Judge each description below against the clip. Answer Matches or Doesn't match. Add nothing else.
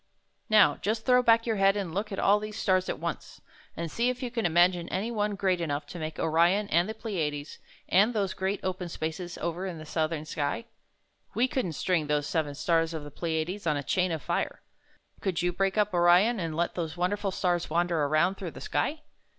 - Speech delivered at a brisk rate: Matches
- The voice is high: Doesn't match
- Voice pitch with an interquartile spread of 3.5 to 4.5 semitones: Matches